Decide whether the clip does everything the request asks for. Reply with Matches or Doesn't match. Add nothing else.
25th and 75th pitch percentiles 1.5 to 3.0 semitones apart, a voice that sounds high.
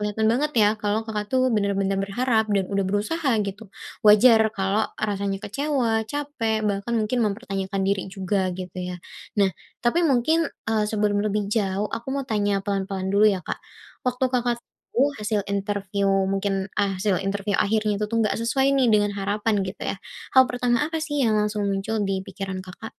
Matches